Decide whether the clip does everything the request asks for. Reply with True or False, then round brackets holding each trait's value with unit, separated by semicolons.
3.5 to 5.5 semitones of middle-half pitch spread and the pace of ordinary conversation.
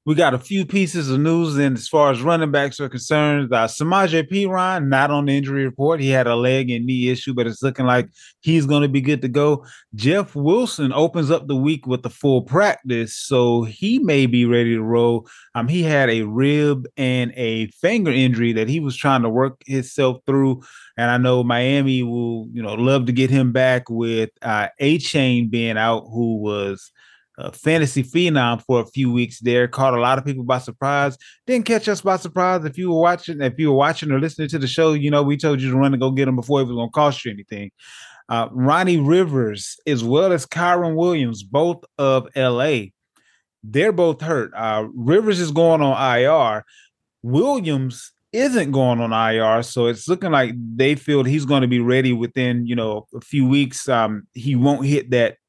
False (4.0 semitones; 210 wpm)